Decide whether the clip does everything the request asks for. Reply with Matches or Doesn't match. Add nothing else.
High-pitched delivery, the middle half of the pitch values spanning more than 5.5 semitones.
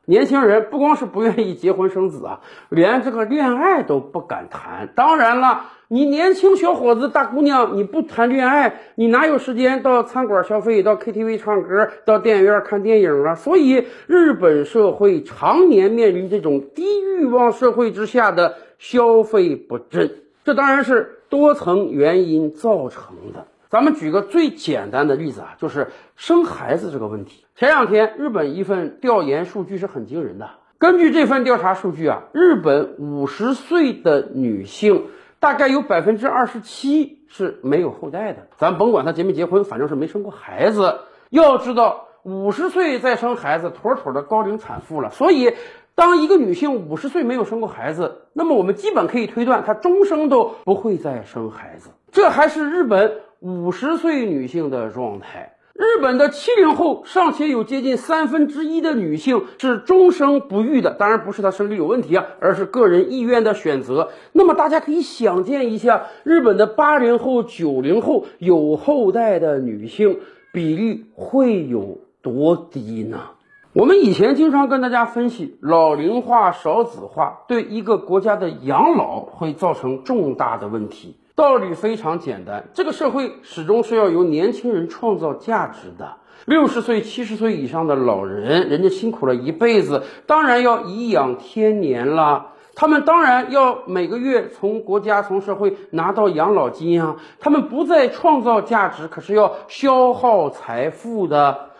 Matches